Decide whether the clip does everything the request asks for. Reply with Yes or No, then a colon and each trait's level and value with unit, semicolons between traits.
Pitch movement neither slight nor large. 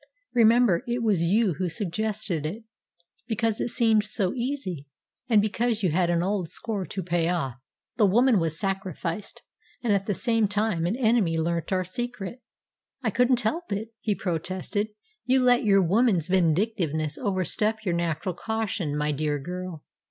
Yes: average, 4.6 semitones